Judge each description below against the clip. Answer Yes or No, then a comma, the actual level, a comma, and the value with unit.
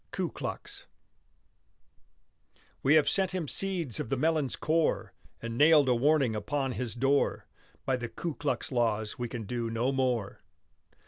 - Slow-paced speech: No, average, 150 wpm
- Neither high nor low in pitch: No, low, 130 Hz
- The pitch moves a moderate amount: Yes, average, 4.3 semitones